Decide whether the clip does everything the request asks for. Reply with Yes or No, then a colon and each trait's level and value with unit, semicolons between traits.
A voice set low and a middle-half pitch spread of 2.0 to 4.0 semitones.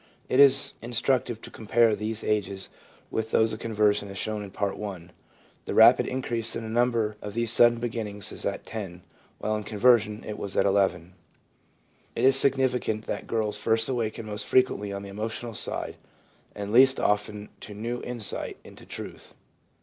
Yes: low, 110 Hz; narrow, 2.4 semitones